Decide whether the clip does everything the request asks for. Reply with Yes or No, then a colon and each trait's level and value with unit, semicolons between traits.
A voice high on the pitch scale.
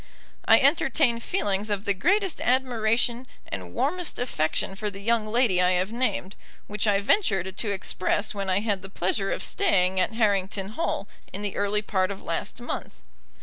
Yes: high, 205 Hz